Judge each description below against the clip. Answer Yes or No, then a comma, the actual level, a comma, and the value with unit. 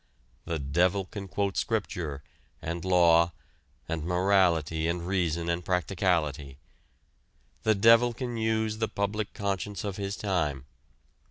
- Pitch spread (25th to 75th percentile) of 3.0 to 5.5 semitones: Yes, average, 3.4 semitones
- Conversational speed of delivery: No, slow, 120 wpm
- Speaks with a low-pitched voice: Yes, very low, 90 Hz